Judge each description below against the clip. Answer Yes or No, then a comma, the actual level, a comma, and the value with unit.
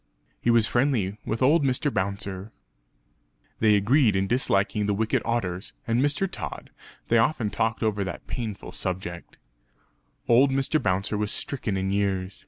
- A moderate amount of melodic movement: Yes, average, 4.0 semitones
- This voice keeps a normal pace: Yes, average, 150 wpm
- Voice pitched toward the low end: Yes, low, 110 Hz